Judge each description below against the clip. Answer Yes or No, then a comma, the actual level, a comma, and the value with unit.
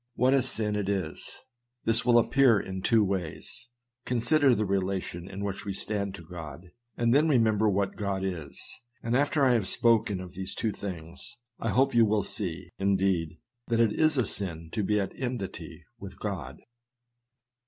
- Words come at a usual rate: Yes, average, 175 wpm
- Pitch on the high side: No, low, 105 Hz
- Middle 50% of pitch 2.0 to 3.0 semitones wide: No, average, 3.8 semitones